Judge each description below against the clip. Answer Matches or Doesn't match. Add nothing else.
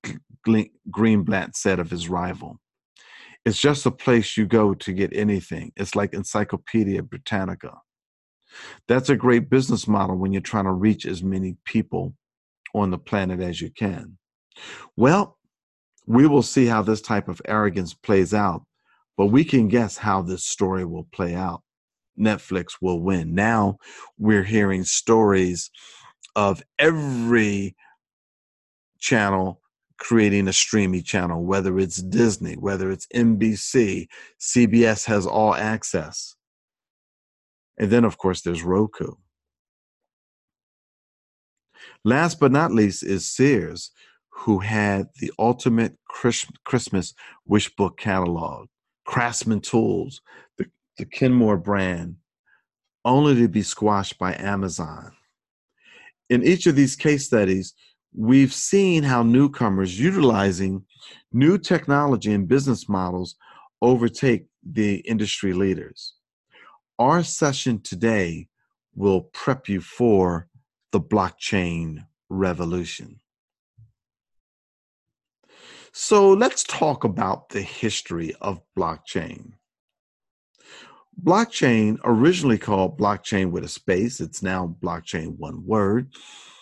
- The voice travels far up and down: Doesn't match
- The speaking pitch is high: Doesn't match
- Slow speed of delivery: Matches